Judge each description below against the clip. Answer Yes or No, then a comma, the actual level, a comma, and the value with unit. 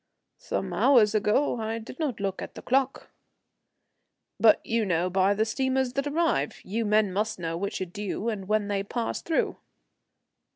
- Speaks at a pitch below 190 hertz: No, high, 215 Hz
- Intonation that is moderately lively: Yes, average, 3.8 semitones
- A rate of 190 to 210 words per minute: No, average, 170 wpm